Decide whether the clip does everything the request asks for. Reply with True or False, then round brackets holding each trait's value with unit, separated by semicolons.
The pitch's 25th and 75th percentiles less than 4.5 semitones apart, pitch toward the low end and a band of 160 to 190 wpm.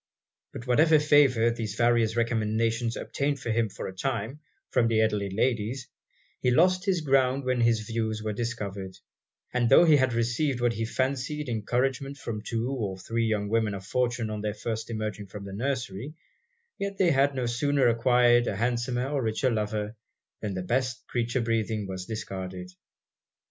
True (3.2 semitones; 115 Hz; 170 wpm)